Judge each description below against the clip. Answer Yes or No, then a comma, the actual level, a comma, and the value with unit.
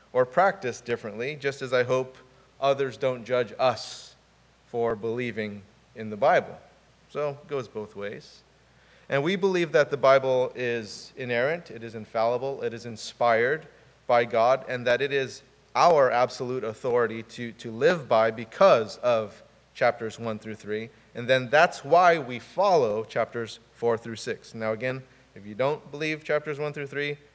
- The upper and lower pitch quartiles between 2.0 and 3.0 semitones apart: No, average, 3.4 semitones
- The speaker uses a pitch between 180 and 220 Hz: No, low, 125 Hz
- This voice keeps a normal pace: Yes, average, 160 wpm